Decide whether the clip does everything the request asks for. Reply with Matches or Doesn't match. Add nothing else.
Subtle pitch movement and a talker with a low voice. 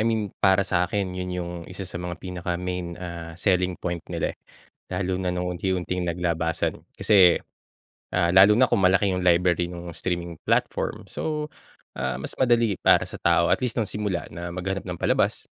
Matches